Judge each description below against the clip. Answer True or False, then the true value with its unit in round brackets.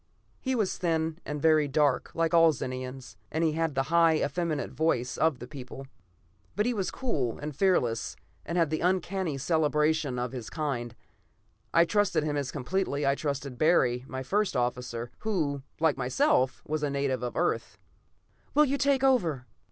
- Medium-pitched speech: True (150 Hz)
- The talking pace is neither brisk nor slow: True (170 wpm)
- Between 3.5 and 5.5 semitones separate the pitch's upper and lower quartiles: True (4.4 semitones)